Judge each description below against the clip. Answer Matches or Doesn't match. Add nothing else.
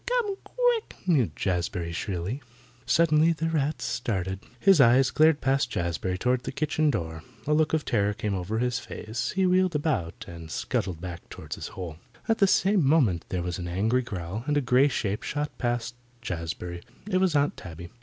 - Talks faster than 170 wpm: Matches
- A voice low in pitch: Matches